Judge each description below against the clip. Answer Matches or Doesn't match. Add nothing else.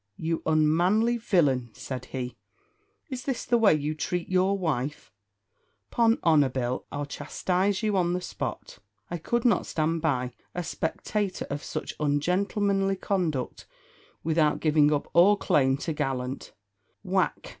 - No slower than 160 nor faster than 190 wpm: Doesn't match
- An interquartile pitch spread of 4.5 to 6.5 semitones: Matches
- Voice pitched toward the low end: Doesn't match